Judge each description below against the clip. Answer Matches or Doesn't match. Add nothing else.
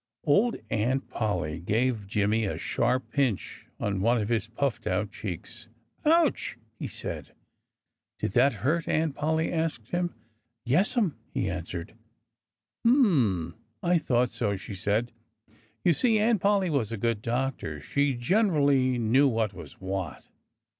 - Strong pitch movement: Matches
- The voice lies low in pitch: Matches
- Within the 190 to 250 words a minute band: Doesn't match